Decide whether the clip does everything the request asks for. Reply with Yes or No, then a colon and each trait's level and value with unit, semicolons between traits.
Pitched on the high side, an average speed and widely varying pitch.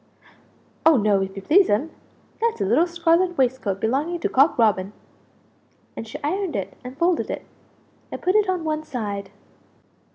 Yes: very high, 280 Hz; average, 165 wpm; wide, 8.5 semitones